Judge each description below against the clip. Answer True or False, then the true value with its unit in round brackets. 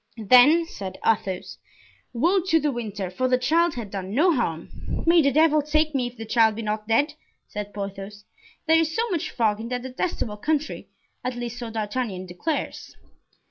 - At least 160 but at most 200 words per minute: True (180 wpm)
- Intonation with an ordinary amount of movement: False (6.6 semitones)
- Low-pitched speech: False (245 Hz)